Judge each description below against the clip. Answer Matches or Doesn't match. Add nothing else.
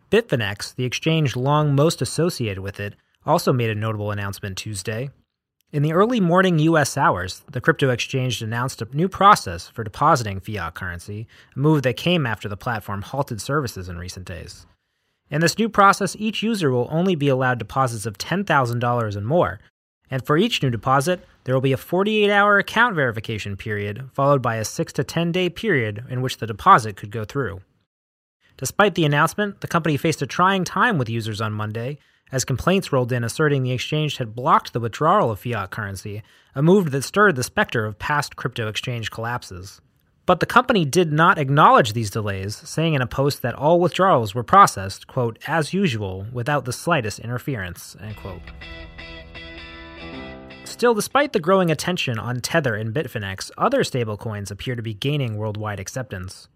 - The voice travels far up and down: Matches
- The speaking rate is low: Doesn't match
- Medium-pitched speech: Doesn't match